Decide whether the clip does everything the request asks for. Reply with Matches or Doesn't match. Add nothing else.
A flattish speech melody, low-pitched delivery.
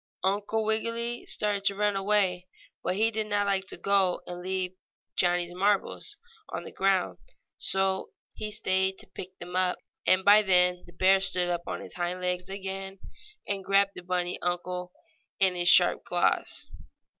Doesn't match